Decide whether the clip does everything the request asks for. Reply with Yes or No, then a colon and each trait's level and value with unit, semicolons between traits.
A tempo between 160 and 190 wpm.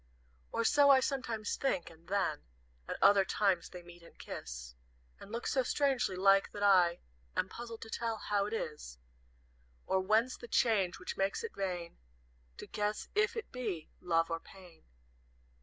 Yes: average, 170 wpm